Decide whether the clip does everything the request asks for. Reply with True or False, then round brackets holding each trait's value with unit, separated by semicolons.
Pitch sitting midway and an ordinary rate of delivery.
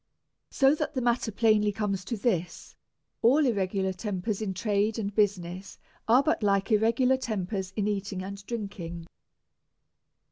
False (205 Hz; 150 wpm)